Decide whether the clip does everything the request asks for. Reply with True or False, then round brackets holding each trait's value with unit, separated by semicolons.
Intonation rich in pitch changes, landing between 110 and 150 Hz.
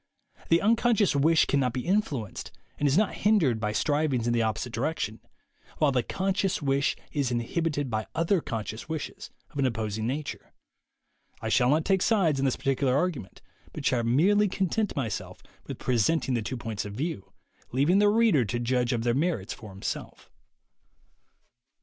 True (6.2 semitones; 140 Hz)